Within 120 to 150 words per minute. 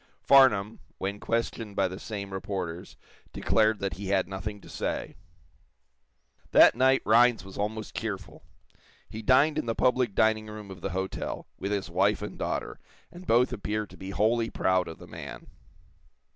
No: average, 165 wpm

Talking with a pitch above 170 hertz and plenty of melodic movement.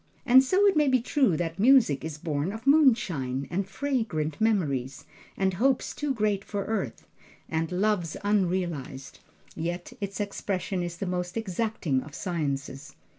Yes: high, 190 Hz; wide, 5.8 semitones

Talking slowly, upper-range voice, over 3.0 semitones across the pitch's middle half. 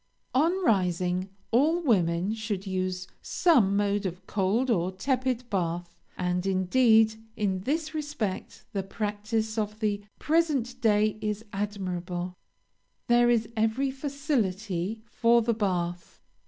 Yes: slow, 120 wpm; high, 210 Hz; average, 4.4 semitones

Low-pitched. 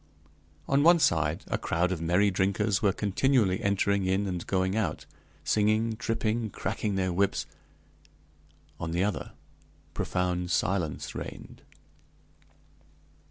Yes: very low, 95 Hz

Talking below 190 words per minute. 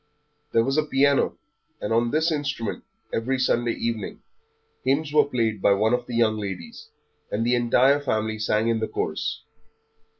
Yes: average, 165 wpm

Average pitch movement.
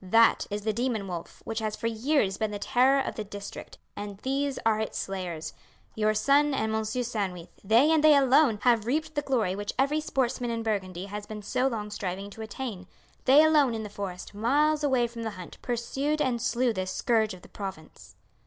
Yes: average, 4.6 semitones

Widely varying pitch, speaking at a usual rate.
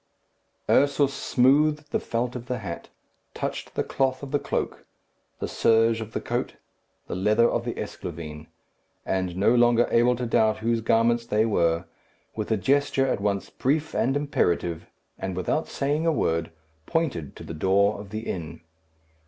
Yes: wide, 5.7 semitones; average, 165 wpm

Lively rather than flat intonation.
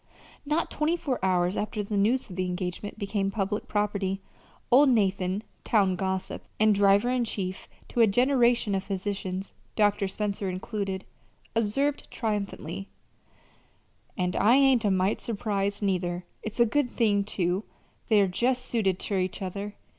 No: average, 3.0 semitones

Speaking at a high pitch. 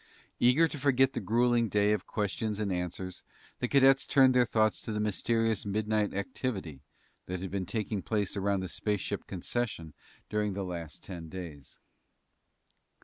No: low, 105 Hz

